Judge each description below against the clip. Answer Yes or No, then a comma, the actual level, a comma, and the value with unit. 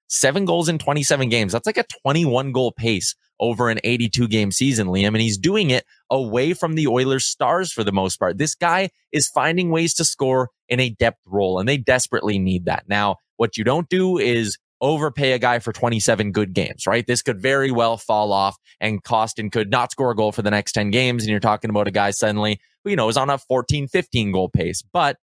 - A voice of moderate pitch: No, low, 120 Hz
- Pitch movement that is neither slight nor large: Yes, average, 4.6 semitones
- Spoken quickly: Yes, fast, 230 wpm